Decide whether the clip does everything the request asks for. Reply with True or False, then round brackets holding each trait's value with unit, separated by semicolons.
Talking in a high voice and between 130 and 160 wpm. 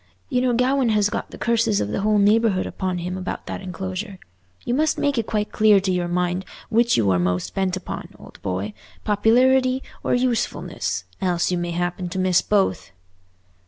False (195 Hz; 180 wpm)